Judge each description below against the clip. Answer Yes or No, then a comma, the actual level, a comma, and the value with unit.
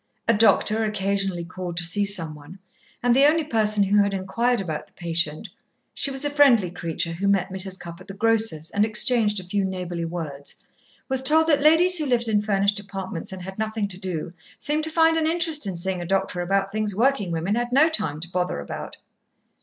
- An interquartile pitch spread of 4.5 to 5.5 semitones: Yes, average, 5.0 semitones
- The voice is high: Yes, high, 200 Hz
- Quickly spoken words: Yes, fast, 210 wpm